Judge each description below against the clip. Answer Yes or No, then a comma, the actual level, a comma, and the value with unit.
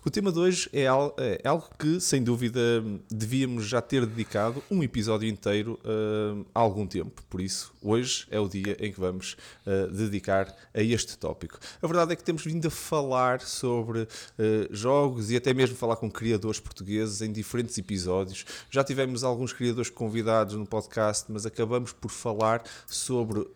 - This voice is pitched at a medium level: No, low, 115 Hz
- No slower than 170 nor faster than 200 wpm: Yes, average, 175 wpm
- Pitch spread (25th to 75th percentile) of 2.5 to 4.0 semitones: Yes, average, 3.1 semitones